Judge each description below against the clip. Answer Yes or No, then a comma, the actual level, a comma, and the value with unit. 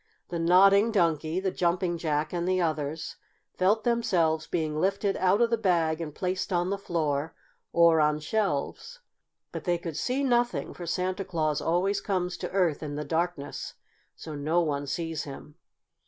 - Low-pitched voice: No, medium, 175 Hz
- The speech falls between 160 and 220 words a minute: Yes, average, 170 wpm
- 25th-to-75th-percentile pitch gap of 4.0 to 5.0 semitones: No, average, 3.4 semitones